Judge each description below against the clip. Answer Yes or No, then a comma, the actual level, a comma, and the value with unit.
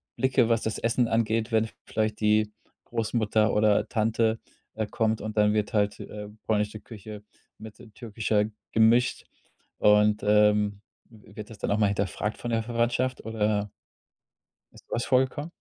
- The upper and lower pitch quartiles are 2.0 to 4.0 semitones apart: No, narrow, 1.5 semitones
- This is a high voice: No, low, 110 Hz